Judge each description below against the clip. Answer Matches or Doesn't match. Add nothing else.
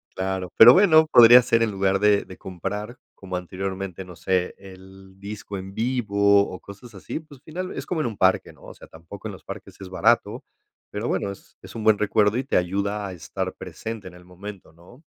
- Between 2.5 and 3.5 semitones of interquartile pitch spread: Matches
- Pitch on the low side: Matches